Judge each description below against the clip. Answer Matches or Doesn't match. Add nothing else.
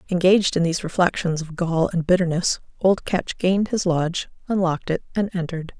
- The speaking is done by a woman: Matches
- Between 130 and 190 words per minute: Matches